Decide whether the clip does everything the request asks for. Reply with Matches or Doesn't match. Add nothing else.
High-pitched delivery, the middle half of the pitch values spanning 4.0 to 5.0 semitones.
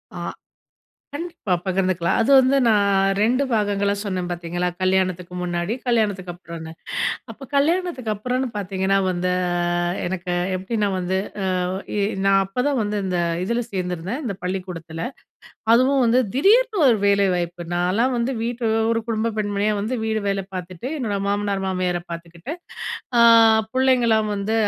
Matches